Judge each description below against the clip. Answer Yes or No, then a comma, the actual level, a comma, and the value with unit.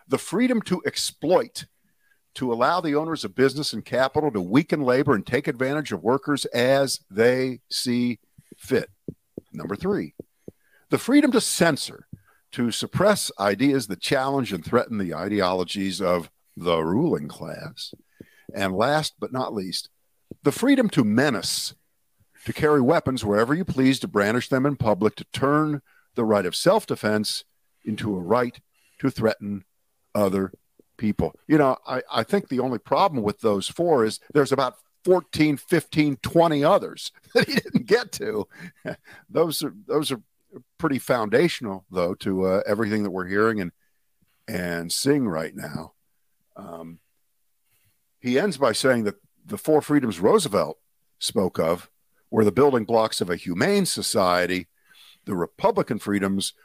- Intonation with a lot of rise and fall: Yes, wide, 6.6 semitones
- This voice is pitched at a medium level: No, low, 130 Hz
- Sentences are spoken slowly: No, average, 150 wpm